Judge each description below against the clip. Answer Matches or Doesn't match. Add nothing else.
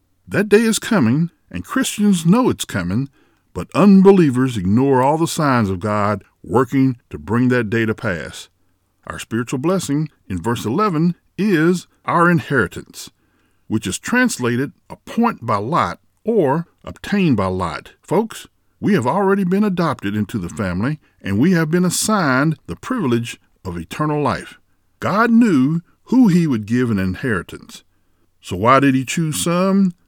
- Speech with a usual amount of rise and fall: Doesn't match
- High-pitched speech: Doesn't match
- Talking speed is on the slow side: Doesn't match